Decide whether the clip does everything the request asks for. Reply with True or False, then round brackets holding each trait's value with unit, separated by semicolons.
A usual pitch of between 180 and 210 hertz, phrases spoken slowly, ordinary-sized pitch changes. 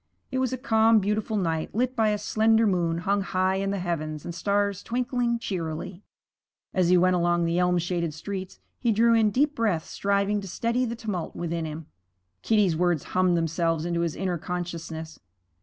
False (185 Hz; 185 wpm; 4.4 semitones)